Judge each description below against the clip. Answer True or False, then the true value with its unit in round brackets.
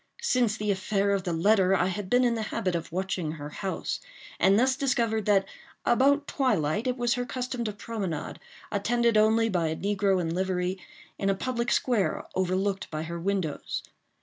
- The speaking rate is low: False (180 wpm)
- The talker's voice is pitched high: True (200 Hz)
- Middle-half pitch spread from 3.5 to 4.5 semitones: True (4.1 semitones)